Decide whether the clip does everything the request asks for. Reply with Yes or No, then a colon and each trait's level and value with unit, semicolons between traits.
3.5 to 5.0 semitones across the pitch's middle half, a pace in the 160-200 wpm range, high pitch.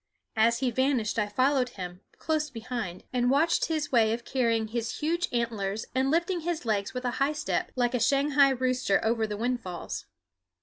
Yes: average, 3.9 semitones; average, 180 wpm; high, 245 Hz